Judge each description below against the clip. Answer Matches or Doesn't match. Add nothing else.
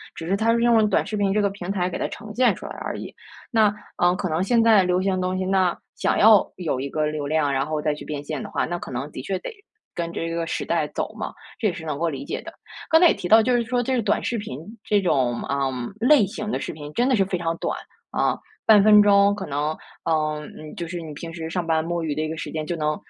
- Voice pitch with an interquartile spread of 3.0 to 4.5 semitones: Doesn't match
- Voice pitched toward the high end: Doesn't match